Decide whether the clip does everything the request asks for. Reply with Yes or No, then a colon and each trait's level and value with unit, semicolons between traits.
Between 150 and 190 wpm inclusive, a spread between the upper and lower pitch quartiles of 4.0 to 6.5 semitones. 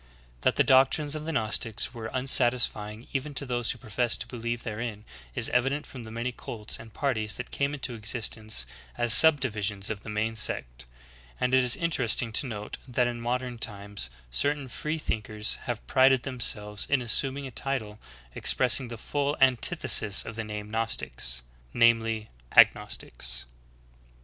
No: average, 165 wpm; average, 3.4 semitones